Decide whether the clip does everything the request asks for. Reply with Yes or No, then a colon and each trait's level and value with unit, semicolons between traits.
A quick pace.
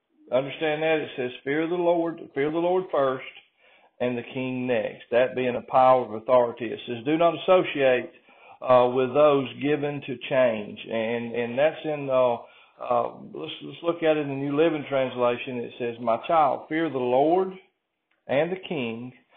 No: average, 180 wpm